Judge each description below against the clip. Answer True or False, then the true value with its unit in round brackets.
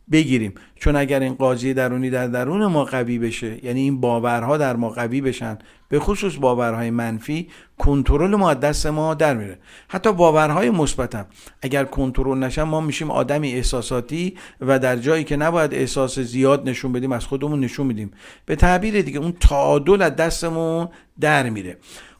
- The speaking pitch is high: False (135 Hz)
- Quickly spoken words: True (165 wpm)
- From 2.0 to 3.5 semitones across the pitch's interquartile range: False (3.9 semitones)